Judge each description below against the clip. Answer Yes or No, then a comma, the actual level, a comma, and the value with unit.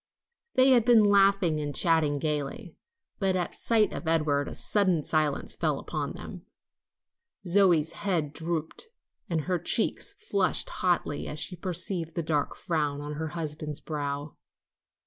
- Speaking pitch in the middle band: Yes, medium, 165 Hz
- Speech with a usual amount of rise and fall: Yes, average, 3.9 semitones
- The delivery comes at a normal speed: Yes, average, 145 wpm